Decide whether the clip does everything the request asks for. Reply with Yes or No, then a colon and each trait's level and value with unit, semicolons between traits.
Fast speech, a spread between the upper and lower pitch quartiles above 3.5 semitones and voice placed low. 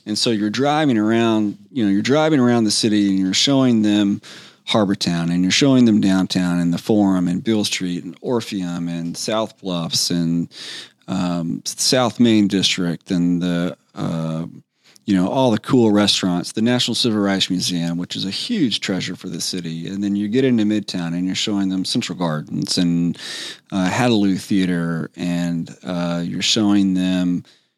No: average, 175 wpm; average, 4.0 semitones; very low, 95 Hz